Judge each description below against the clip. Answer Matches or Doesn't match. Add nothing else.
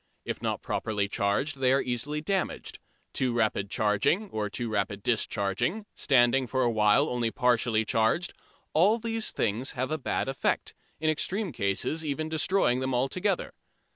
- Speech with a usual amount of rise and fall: Doesn't match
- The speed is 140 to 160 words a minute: Matches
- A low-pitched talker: Matches